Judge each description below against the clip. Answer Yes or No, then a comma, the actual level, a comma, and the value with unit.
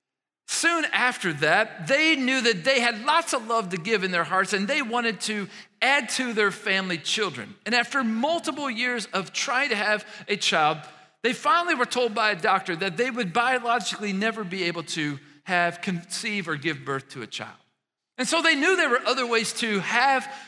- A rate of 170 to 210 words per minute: Yes, average, 200 wpm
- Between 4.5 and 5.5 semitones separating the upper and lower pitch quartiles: Yes, average, 5.2 semitones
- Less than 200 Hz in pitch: No, high, 225 Hz